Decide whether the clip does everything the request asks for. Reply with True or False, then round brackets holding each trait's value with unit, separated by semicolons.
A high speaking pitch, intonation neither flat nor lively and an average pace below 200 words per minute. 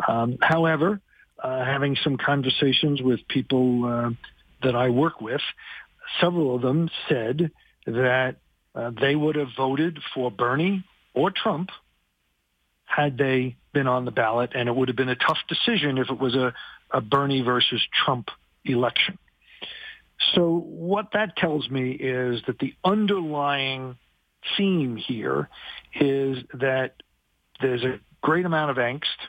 False (135 Hz; 3.4 semitones; 140 wpm)